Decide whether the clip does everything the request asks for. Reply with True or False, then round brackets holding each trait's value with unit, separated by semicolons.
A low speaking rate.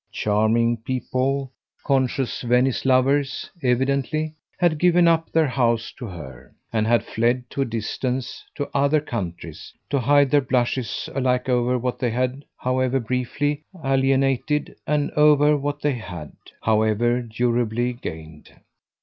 True (130 wpm)